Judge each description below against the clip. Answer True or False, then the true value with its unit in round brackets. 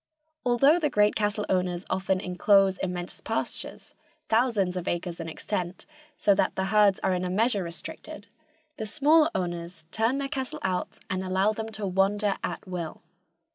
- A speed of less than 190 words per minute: True (165 wpm)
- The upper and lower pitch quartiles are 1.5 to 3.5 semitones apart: True (3.2 semitones)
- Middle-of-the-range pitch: False (195 Hz)